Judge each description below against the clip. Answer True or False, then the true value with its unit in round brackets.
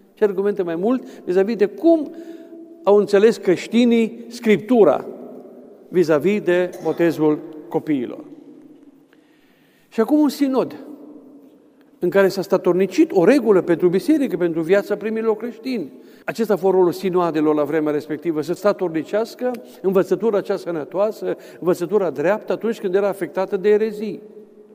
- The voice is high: True (205 Hz)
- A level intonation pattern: False (4.9 semitones)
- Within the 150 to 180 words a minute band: False (130 wpm)